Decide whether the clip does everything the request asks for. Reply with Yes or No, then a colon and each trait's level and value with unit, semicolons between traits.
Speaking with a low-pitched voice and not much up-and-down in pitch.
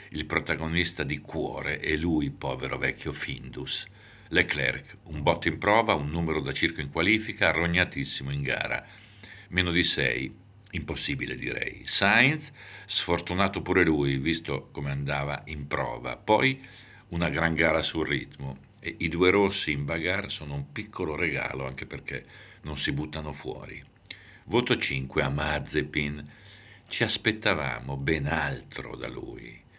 No: very low, 85 Hz; wide, 5.5 semitones